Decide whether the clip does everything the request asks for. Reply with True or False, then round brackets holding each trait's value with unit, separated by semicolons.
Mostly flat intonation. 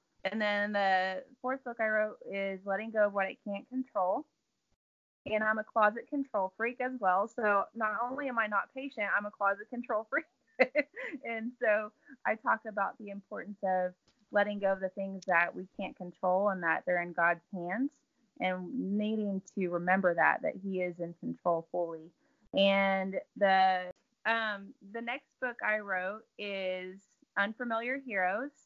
False (3.8 semitones)